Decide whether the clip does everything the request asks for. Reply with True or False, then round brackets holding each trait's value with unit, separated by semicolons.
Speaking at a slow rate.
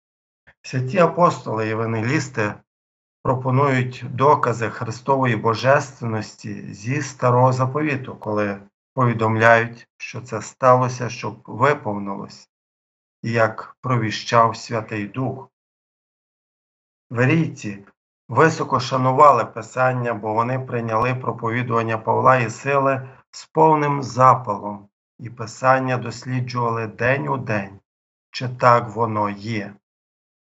True (90 wpm)